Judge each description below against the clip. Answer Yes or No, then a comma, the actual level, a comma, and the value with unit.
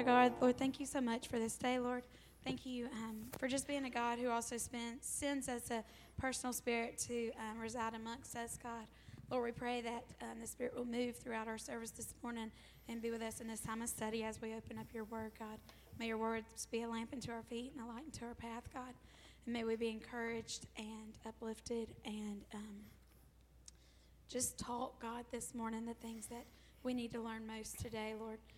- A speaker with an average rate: No, fast, 215 wpm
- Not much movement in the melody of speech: Yes, narrow, 1.5 semitones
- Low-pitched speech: No, high, 230 Hz